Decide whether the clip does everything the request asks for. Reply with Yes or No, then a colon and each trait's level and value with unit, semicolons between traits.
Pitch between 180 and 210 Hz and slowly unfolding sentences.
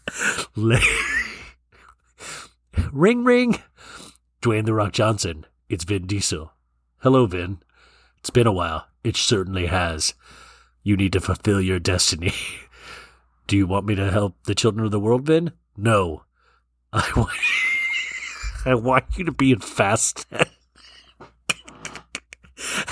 No: low, 100 Hz; slow, 120 wpm